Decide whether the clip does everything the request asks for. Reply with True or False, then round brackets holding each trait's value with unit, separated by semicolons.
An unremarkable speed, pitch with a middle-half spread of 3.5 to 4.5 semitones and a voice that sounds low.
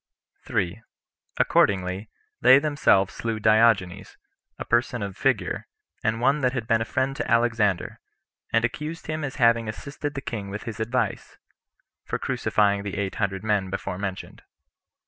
True (150 wpm; 3.8 semitones; 110 Hz)